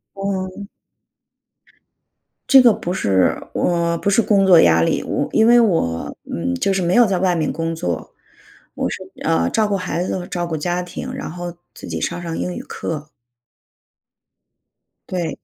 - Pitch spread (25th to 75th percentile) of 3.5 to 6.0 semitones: No, average, 3.1 semitones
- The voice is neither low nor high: Yes, medium, 175 Hz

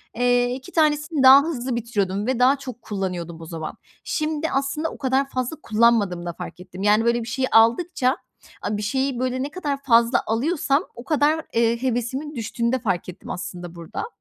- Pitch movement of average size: Yes, average, 4.5 semitones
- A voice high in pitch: Yes, high, 245 Hz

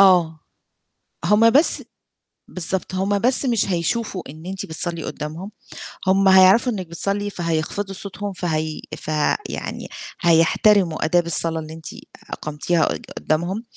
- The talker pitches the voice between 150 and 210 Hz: Yes, medium, 185 Hz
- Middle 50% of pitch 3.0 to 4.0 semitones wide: Yes, average, 3.6 semitones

